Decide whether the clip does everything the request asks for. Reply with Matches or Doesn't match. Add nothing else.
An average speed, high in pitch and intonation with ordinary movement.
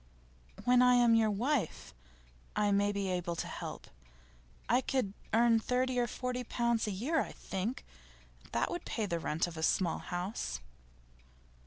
Matches